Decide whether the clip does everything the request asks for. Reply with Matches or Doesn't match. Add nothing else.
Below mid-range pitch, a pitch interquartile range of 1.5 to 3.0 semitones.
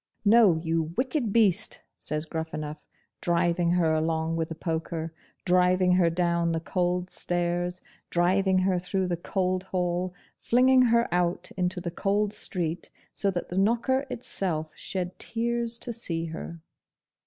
Doesn't match